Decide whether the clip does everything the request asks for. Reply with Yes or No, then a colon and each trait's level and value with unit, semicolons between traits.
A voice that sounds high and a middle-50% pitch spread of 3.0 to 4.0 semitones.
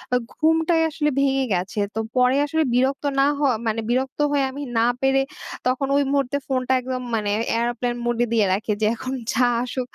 No: very high, 260 Hz; narrow, 2.6 semitones